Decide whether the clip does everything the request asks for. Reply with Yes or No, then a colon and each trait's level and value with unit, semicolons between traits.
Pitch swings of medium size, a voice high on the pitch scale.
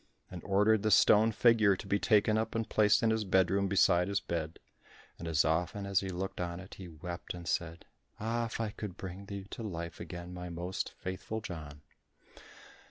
No: average, 3.4 semitones; very low, 95 Hz